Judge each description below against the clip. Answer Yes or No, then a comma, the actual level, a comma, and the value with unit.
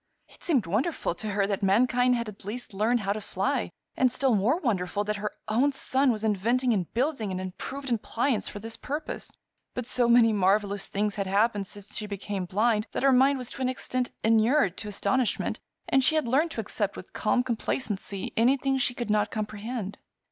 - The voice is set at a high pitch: Yes, high, 225 Hz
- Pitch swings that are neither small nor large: Yes, average, 3.8 semitones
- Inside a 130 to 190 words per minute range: No, average, 200 wpm